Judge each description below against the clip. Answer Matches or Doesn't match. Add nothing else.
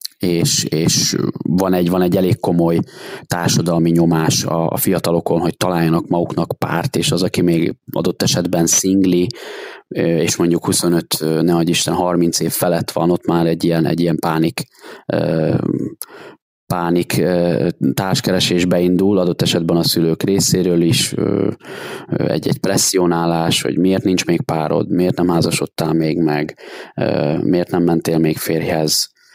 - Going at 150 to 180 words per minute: Doesn't match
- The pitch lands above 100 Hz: Doesn't match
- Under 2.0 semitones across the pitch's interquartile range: Matches